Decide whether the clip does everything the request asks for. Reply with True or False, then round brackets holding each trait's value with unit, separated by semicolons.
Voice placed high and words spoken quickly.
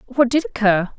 False (245 Hz; 185 wpm)